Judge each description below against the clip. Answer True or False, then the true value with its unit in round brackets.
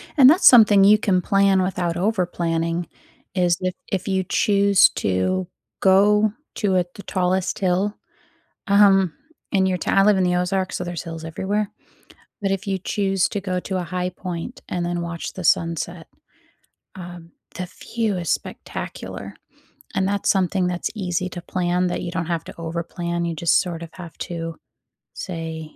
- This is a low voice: False (185 Hz)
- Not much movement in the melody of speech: True (2.2 semitones)